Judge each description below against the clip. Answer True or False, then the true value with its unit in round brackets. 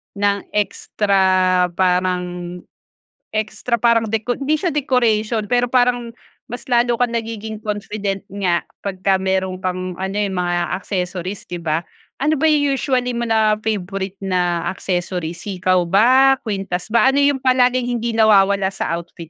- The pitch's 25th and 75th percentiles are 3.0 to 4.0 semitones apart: False (4.4 semitones)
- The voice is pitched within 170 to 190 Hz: False (205 Hz)